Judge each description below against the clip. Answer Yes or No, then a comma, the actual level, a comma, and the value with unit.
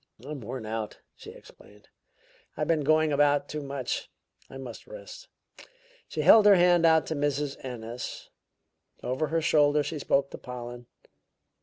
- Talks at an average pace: Yes, average, 150 wpm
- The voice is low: No, medium, 145 Hz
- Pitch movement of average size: Yes, average, 4.0 semitones